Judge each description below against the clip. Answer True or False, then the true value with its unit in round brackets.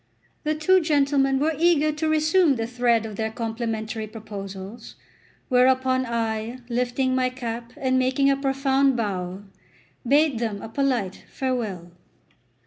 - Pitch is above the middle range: True (255 Hz)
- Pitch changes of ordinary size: True (3.7 semitones)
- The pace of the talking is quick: False (135 wpm)